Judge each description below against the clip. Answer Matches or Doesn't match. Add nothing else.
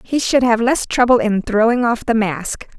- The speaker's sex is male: Doesn't match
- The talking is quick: Matches